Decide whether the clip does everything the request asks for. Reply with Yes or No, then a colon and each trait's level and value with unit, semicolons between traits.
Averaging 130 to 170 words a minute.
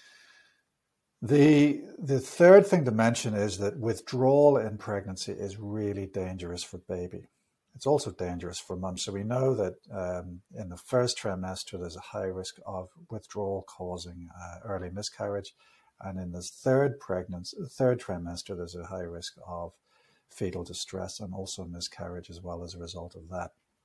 Yes: average, 160 wpm